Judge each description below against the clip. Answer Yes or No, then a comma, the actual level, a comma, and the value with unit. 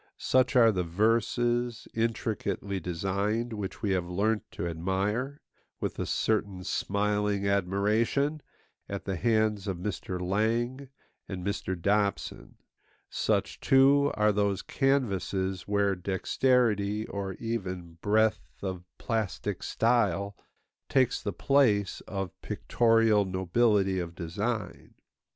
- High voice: No, low, 105 Hz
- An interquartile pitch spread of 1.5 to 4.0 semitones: Yes, average, 3.2 semitones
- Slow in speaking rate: Yes, slow, 110 wpm